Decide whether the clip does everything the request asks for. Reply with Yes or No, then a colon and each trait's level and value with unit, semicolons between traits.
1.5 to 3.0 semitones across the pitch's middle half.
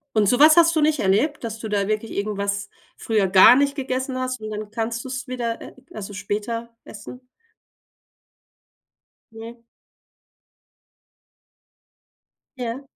No: average, 3.5 semitones